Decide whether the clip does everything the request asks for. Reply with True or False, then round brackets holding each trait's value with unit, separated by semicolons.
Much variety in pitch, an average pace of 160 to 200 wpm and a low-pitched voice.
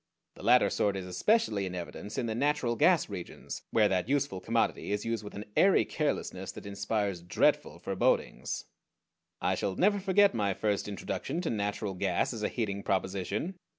True (6.5 semitones; 175 wpm; 105 Hz)